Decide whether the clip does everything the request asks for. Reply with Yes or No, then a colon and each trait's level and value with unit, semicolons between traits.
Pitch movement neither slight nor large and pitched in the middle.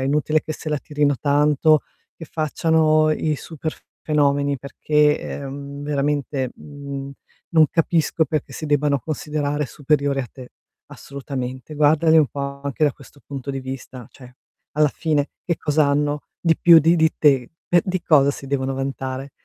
No: narrow, 1.8 semitones; medium, 145 Hz